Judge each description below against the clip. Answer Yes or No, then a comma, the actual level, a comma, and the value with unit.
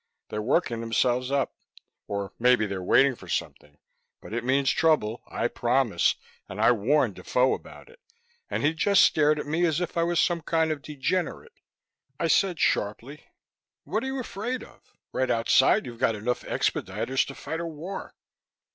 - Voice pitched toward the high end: No, low, 135 Hz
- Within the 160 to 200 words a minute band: Yes, average, 175 wpm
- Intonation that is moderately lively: No, wide, 5.7 semitones